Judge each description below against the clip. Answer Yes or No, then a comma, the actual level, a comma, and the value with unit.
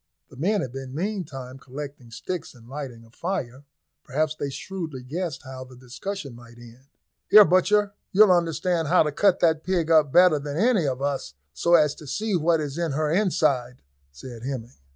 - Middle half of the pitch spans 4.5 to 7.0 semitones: Yes, wide, 5.4 semitones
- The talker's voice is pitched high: No, medium, 150 Hz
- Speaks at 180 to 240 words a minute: Yes, average, 185 wpm